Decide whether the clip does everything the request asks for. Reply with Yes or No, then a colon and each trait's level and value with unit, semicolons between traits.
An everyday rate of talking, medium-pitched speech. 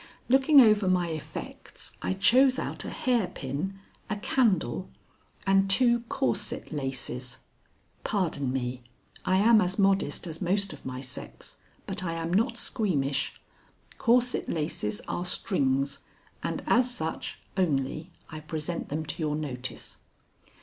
No: slow, 130 wpm; medium, 175 Hz